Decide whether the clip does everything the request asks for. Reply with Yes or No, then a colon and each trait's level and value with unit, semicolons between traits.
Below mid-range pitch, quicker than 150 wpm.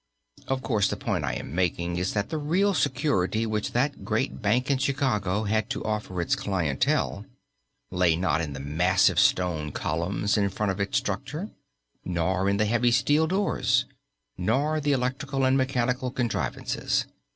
Yes: low, 105 Hz; average, 160 wpm